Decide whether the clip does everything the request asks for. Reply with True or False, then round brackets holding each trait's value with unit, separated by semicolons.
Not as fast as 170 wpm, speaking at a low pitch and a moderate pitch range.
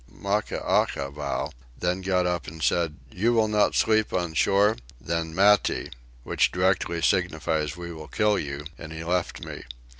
True (150 wpm; 90 Hz; 3.6 semitones)